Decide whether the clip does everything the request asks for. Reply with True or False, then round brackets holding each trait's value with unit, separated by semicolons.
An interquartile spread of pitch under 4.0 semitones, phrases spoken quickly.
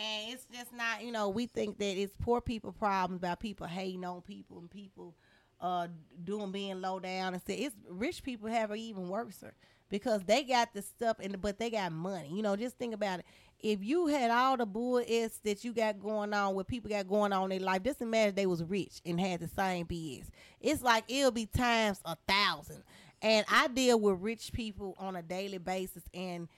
True (3.5 semitones; 225 wpm)